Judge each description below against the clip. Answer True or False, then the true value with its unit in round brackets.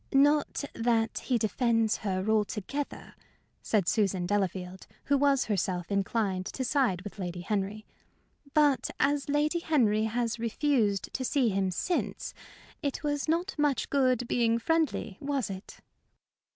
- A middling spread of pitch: False (6.0 semitones)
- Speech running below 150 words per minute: True (135 wpm)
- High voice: True (230 Hz)